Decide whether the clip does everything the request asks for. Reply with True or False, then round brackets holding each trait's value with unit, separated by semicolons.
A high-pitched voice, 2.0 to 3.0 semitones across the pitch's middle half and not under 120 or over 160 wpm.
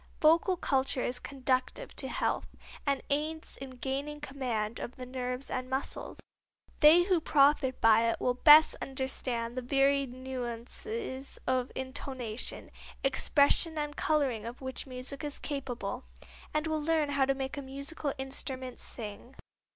True (265 Hz; 2.6 semitones; 145 wpm)